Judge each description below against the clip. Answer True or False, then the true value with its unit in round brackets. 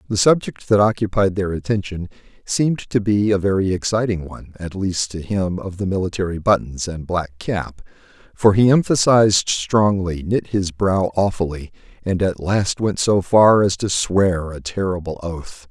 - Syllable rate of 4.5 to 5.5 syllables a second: True (4.6 syllables/s)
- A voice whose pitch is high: False (95 Hz)